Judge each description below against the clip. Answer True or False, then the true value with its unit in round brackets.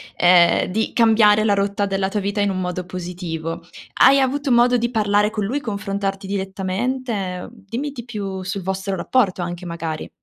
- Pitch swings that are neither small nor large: True (3.3 semitones)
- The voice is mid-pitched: False (200 Hz)